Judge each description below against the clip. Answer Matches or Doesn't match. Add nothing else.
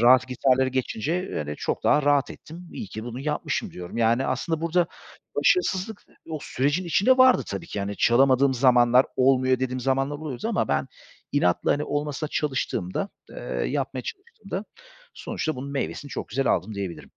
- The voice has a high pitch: Doesn't match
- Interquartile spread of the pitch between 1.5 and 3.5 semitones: Doesn't match